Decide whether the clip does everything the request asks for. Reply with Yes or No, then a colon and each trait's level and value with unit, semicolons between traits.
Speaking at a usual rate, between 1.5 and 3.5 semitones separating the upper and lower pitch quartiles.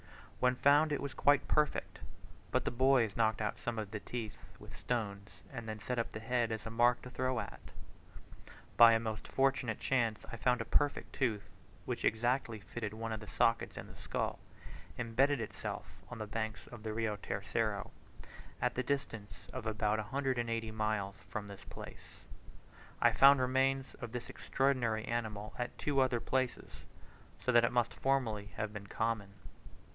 Yes: average, 175 wpm; average, 2.9 semitones